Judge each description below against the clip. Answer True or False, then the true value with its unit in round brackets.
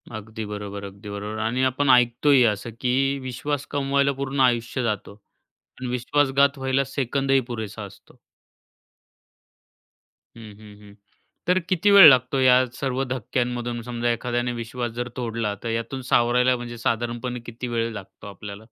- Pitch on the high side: False (120 Hz)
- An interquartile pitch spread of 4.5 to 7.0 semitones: False (2.7 semitones)